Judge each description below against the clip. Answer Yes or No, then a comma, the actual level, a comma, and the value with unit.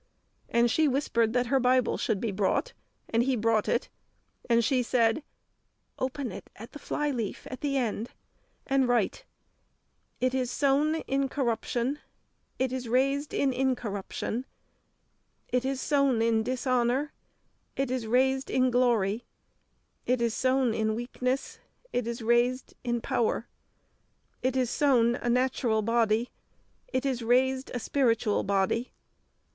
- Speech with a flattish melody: Yes, narrow, 2.2 semitones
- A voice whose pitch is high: Yes, very high, 250 Hz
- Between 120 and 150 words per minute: Yes, average, 140 wpm